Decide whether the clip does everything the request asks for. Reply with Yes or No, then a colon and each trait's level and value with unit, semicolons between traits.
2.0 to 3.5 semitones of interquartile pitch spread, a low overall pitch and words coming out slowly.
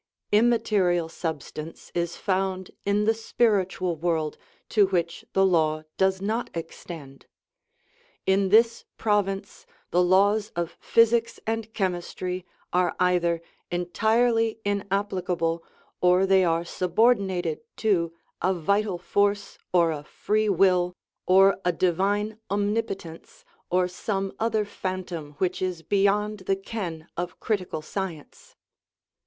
No: average, 2.9 semitones; high, 190 Hz; slow, 130 wpm